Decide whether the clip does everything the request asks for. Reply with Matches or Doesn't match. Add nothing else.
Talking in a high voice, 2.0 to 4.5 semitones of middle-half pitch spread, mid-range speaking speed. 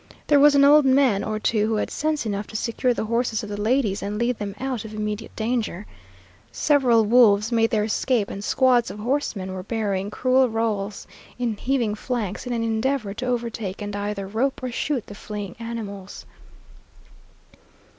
Matches